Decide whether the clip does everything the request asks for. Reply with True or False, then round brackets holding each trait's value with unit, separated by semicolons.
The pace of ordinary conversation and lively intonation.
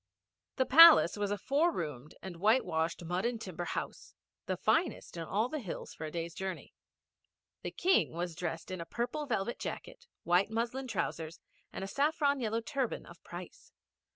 True (175 wpm; 7.3 semitones)